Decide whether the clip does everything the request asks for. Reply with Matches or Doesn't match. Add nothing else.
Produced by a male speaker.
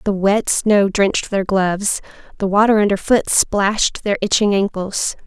Doesn't match